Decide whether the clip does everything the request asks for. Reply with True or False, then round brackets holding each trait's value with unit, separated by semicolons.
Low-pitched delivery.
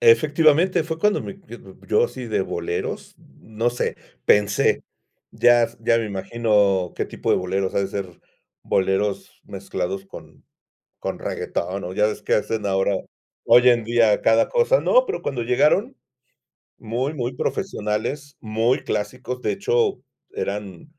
True (115 Hz)